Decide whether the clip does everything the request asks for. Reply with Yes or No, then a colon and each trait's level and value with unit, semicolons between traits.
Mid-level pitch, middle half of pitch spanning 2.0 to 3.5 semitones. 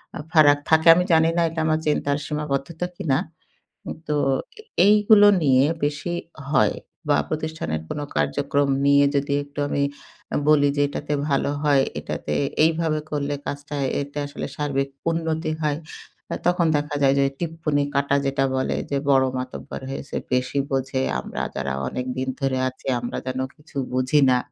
Yes: medium, 145 Hz; narrow, 2.4 semitones